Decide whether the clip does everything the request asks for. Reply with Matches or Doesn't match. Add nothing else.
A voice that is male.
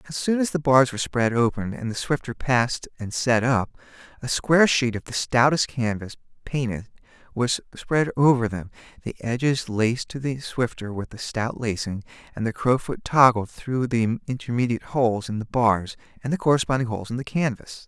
Matches